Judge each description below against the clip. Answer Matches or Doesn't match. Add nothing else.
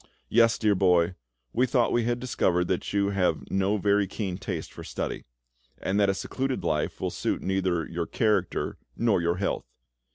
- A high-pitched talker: Doesn't match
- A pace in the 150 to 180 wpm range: Matches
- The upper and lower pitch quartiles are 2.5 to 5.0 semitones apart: Matches